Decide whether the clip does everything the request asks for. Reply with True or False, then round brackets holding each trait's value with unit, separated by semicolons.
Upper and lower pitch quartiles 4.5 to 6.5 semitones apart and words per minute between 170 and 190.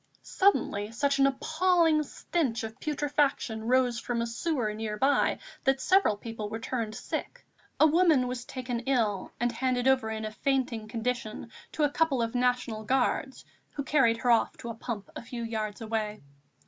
False (3.6 semitones; 175 wpm)